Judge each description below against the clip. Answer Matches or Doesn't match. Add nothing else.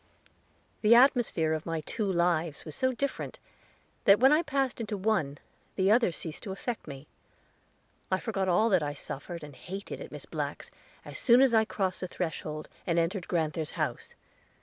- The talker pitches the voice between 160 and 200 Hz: Matches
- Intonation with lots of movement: Matches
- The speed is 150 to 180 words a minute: Matches